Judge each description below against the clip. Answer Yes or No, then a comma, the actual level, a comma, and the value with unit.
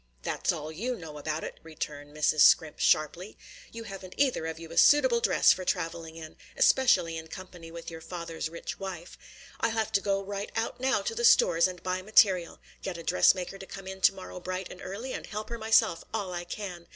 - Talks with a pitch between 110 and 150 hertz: No, medium, 185 Hz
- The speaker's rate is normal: No, fast, 215 wpm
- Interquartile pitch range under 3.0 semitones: No, average, 4.1 semitones